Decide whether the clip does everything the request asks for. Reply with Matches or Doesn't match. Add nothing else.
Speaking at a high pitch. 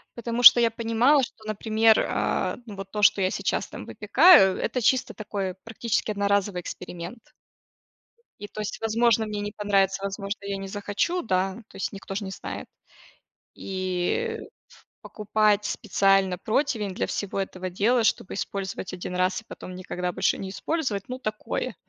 Matches